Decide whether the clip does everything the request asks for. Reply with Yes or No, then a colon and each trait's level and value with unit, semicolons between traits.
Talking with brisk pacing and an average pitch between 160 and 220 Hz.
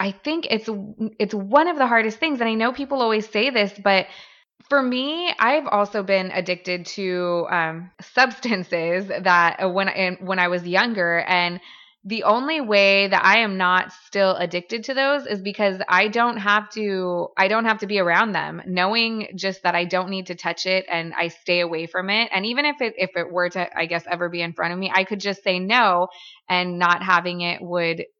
Yes: fast, 210 wpm; high, 190 Hz